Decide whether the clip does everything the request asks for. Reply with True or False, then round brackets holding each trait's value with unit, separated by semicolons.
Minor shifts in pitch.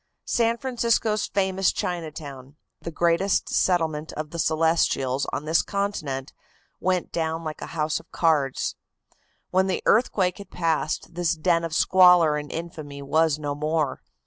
False (3.2 semitones)